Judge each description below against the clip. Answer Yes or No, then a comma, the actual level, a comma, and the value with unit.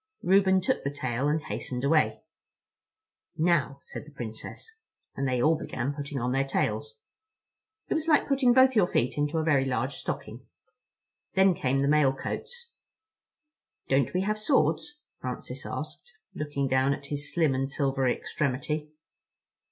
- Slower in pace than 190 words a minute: Yes, average, 150 wpm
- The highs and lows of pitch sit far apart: Yes, wide, 5.9 semitones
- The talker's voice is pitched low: No, medium, 145 Hz